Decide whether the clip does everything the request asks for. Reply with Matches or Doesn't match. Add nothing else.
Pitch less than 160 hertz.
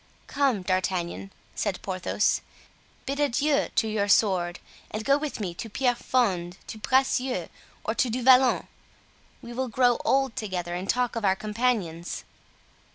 Doesn't match